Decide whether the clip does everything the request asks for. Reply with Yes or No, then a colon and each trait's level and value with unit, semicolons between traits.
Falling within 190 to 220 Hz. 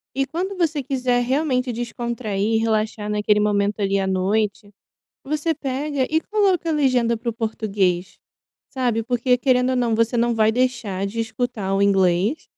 No: high, 235 Hz